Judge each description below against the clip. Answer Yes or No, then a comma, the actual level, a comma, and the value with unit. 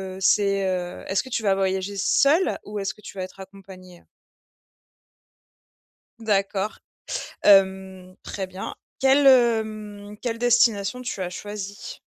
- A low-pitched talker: No, high, 200 Hz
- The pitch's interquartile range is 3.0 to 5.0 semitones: No, narrow, 2.5 semitones